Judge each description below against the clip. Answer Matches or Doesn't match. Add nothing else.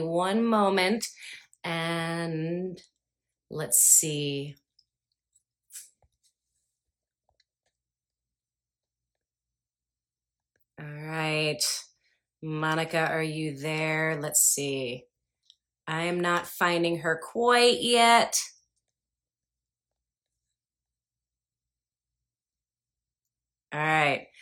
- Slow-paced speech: Matches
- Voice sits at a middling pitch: Matches